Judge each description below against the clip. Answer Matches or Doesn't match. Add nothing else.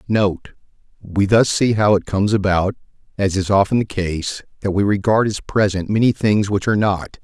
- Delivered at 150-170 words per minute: Doesn't match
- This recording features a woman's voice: Doesn't match